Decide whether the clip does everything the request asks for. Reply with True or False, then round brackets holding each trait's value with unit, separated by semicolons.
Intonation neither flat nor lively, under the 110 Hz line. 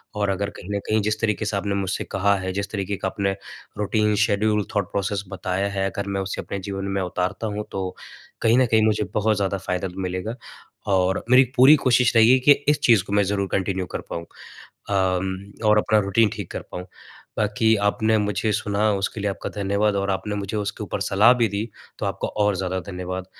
False (1.8 semitones; 100 Hz)